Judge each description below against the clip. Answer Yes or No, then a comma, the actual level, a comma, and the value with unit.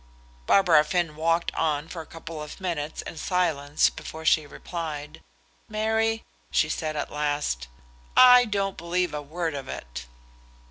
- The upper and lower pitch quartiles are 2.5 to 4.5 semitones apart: Yes, average, 3.4 semitones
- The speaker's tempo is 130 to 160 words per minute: Yes, average, 145 wpm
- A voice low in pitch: No, medium, 160 Hz